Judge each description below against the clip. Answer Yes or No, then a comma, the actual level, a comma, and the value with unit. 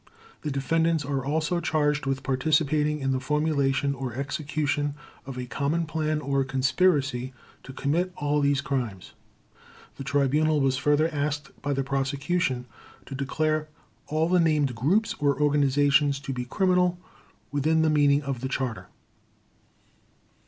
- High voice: No, medium, 145 Hz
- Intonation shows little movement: Yes, narrow, 2.3 semitones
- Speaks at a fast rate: No, average, 140 wpm